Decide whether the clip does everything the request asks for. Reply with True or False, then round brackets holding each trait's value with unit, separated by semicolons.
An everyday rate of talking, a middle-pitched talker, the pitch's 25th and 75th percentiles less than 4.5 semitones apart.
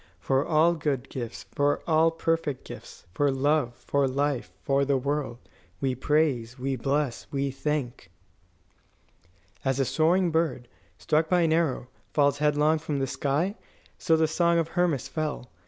True (155 wpm; 145 Hz; 3.0 semitones)